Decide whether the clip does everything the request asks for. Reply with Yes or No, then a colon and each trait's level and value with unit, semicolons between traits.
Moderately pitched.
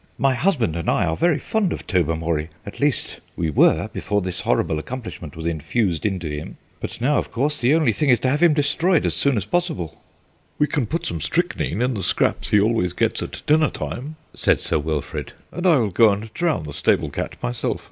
No: low, 110 Hz